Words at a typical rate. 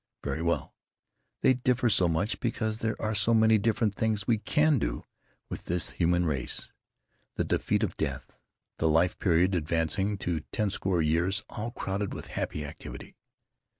Yes: average, 160 wpm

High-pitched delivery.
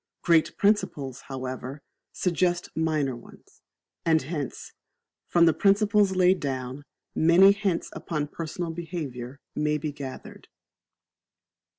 No: medium, 160 Hz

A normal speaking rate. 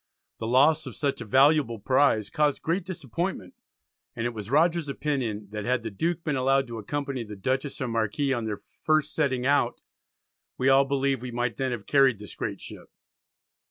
Yes: average, 190 wpm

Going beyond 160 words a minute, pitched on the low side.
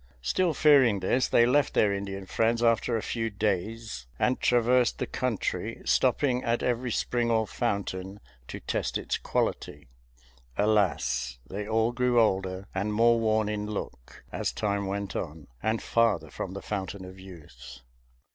No: average, 155 wpm; low, 105 Hz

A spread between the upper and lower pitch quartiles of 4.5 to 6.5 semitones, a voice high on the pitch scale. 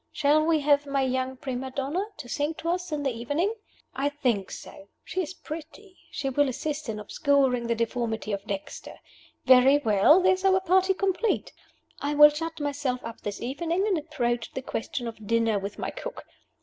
Yes: average, 5.3 semitones; very high, 280 Hz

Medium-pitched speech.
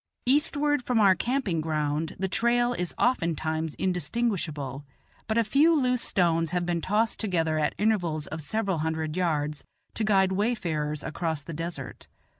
Yes: medium, 175 Hz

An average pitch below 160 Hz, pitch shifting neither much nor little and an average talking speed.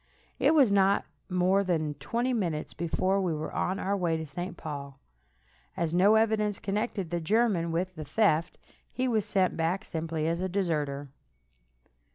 No: medium, 180 Hz; average, 3.8 semitones; average, 165 wpm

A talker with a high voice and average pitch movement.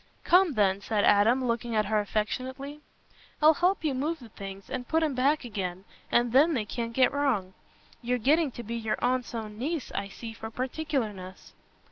Yes: high, 240 Hz; average, 4.9 semitones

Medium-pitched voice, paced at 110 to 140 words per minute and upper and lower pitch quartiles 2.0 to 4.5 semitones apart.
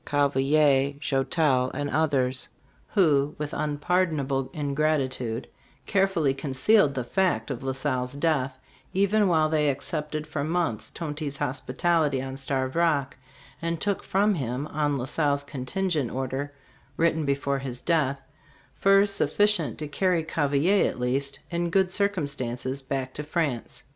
Yes: medium, 145 Hz; slow, 135 wpm; average, 3.7 semitones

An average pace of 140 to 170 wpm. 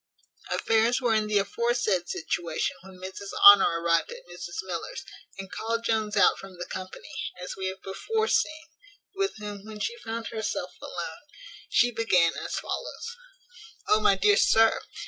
Yes: average, 160 wpm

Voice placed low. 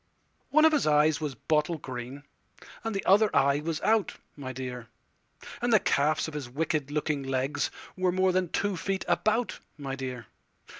No: medium, 150 Hz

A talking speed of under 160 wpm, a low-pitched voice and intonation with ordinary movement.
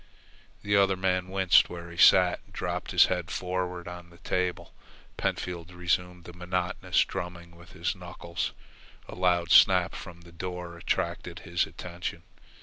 No: average, 150 wpm; very low, 90 Hz; narrow, 1.0 semitones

